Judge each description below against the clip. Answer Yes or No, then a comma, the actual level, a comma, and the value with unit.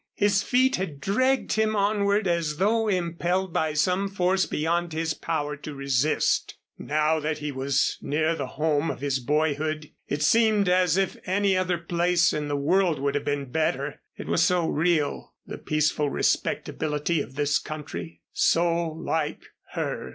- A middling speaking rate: Yes, average, 160 wpm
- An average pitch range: Yes, average, 3.8 semitones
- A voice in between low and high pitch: Yes, medium, 160 Hz